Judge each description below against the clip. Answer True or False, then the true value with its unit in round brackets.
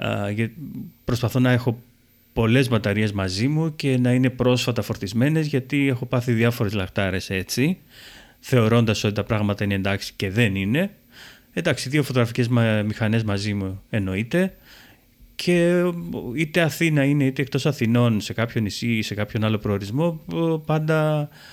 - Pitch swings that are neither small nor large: True (4.6 semitones)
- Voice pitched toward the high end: False (120 Hz)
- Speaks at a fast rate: False (140 wpm)